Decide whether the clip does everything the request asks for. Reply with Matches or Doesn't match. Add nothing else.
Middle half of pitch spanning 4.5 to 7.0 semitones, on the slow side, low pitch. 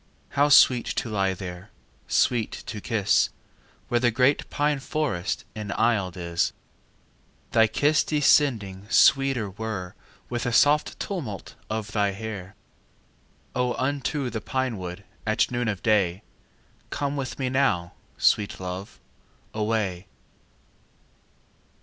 Matches